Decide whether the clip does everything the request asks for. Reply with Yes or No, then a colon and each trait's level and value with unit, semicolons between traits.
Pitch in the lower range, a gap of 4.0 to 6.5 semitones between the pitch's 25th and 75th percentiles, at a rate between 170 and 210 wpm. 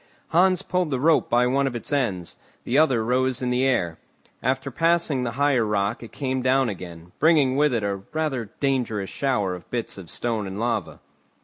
Yes: low, 125 Hz; average, 4.3 semitones; average, 195 wpm